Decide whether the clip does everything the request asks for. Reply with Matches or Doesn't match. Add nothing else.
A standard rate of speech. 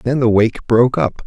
Doesn't match